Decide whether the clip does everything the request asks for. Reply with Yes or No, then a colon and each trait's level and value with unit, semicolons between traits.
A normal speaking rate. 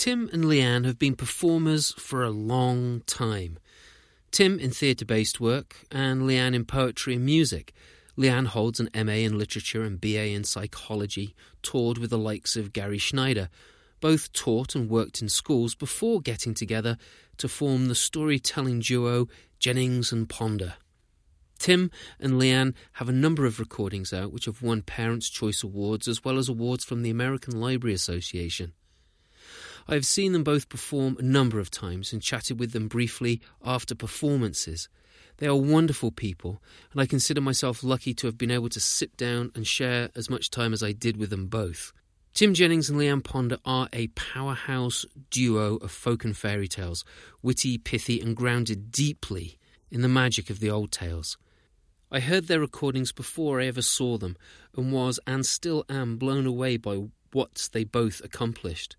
Yes: average, 175 wpm